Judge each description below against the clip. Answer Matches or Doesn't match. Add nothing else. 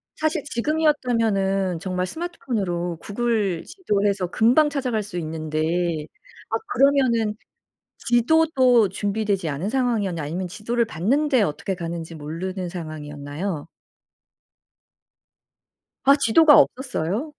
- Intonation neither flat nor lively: Doesn't match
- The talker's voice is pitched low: Doesn't match